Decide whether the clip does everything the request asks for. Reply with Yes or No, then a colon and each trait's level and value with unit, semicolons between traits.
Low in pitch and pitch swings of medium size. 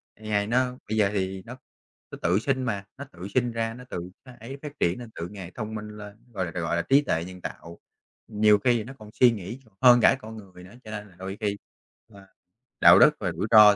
Yes: low, 105 Hz; average, 3.7 semitones